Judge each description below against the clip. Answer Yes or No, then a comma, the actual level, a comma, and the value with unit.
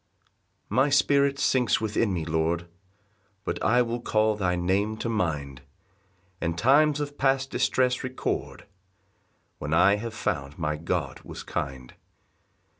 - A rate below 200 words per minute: Yes, slow, 135 wpm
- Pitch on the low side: Yes, low, 105 Hz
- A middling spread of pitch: No, wide, 7.8 semitones